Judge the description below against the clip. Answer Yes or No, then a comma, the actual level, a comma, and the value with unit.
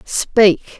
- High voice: Yes, high, 205 Hz